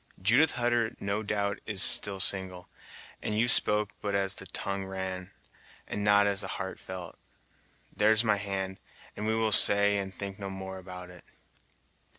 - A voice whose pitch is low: Yes, low, 100 Hz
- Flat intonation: Yes, narrow, 1.7 semitones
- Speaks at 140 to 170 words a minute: Yes, average, 165 wpm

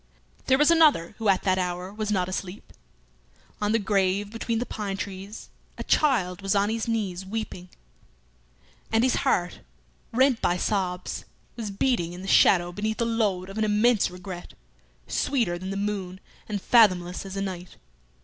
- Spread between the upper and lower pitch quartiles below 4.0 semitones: Yes, average, 3.4 semitones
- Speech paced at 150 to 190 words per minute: Yes, average, 170 wpm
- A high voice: Yes, high, 200 Hz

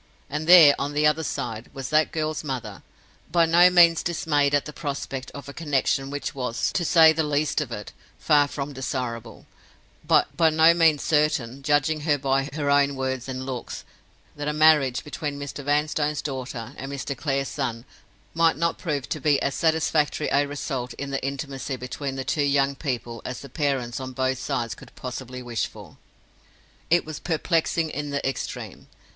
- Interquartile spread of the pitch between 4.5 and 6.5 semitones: No, narrow, 2.6 semitones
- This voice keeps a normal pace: Yes, average, 180 wpm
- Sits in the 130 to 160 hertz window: Yes, medium, 140 Hz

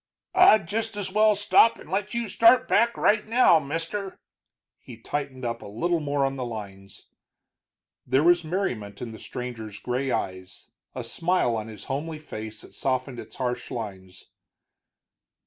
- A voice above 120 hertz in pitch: Yes, medium, 140 Hz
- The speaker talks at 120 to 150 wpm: No, average, 160 wpm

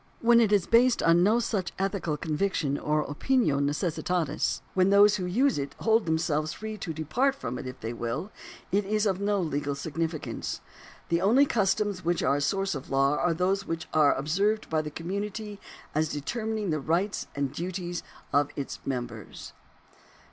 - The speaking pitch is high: No, medium, 175 Hz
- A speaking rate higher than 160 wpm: Yes, average, 180 wpm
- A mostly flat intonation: No, wide, 5.4 semitones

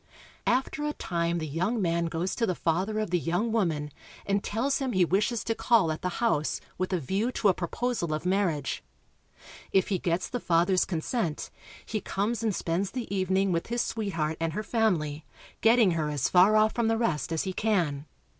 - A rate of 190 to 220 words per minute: Yes, average, 200 wpm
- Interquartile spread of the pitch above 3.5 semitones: Yes, average, 5.0 semitones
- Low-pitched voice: No, high, 190 Hz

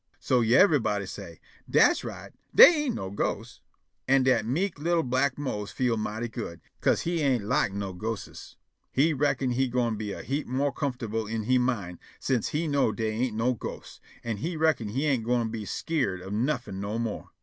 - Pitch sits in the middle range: No, low, 125 Hz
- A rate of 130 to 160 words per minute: No, average, 190 wpm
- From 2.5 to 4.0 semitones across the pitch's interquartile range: No, average, 4.4 semitones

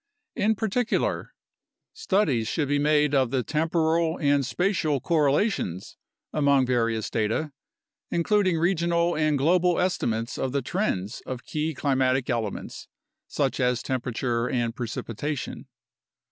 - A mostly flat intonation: No, wide, 5.4 semitones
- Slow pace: Yes, slow, 120 wpm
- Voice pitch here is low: No, medium, 145 Hz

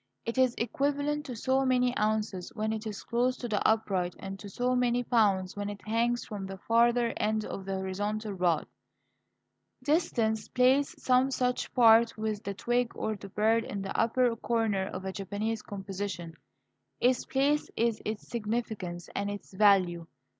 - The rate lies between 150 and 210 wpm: Yes, average, 170 wpm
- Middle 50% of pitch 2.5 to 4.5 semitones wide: Yes, average, 3.4 semitones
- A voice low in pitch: No, high, 220 Hz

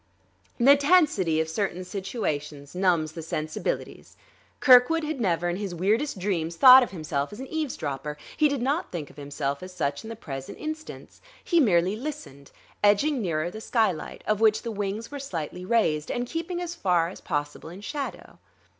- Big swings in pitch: Yes, wide, 8.3 semitones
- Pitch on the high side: Yes, high, 195 Hz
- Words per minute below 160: No, average, 175 wpm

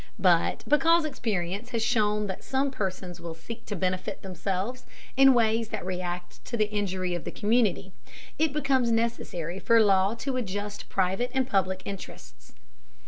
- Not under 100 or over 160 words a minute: Yes, average, 155 wpm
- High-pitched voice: Yes, high, 205 Hz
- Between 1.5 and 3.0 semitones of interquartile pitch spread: No, average, 4.3 semitones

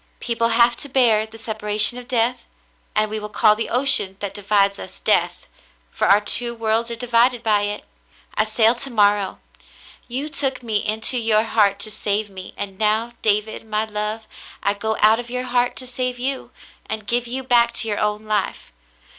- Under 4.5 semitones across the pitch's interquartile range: Yes, narrow, 2.4 semitones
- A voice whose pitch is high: Yes, high, 220 Hz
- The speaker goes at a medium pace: Yes, average, 190 wpm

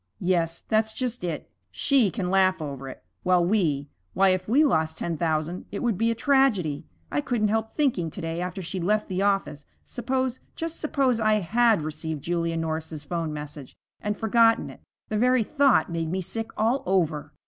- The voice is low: No, medium, 185 Hz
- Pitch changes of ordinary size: No, wide, 5.7 semitones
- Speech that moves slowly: No, average, 185 wpm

